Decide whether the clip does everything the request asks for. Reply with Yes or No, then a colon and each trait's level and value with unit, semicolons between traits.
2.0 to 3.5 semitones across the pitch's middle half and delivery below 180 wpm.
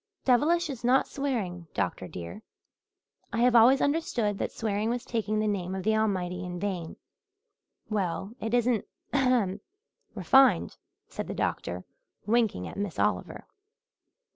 No: average, 4.8 semitones; average, 140 wpm